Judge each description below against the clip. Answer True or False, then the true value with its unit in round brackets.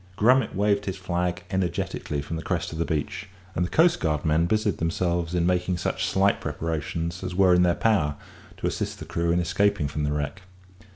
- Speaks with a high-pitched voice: False (90 Hz)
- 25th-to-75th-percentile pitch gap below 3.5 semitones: True (2.9 semitones)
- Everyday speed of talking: True (190 wpm)